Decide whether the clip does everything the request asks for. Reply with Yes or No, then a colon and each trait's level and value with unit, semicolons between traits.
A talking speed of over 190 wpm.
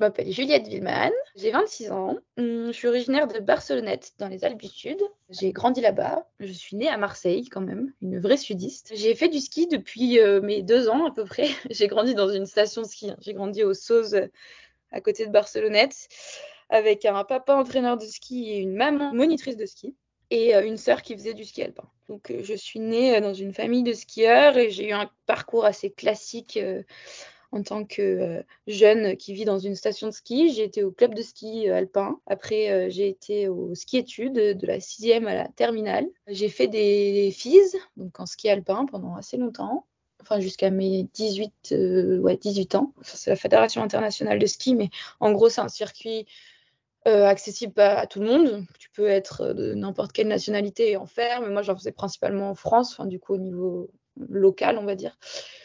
Yes: average, 205 wpm